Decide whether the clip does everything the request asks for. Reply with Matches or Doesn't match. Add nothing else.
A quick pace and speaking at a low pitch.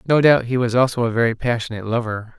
Matches